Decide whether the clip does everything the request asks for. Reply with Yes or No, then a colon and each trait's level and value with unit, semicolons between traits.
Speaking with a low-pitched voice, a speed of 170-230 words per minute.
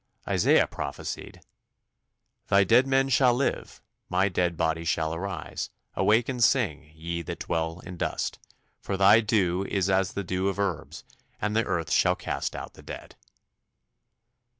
No: very low, 95 Hz; average, 150 wpm